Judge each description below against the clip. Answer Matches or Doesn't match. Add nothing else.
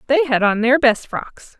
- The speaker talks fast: Matches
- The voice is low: Doesn't match